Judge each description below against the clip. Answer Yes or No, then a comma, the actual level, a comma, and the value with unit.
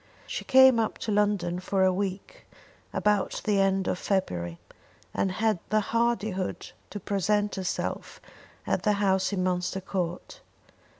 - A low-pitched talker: No, high, 195 Hz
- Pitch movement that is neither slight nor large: No, narrow, 2.1 semitones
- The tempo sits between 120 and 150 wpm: Yes, average, 140 wpm